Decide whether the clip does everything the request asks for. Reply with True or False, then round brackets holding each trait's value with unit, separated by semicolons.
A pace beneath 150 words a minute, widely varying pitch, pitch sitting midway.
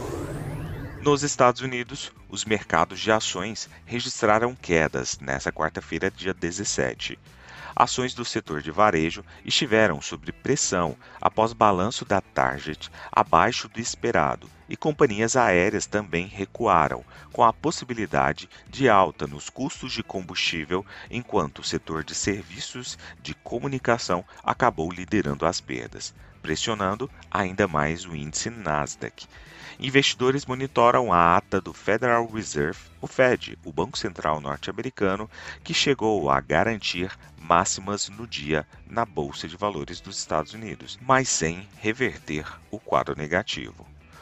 False (125 wpm; 6.3 semitones; 95 Hz)